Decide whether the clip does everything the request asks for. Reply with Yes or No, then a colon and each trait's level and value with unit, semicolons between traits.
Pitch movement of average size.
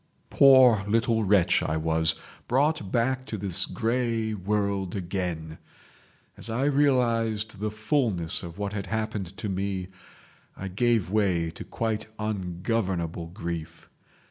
Yes: average, 4.0 semitones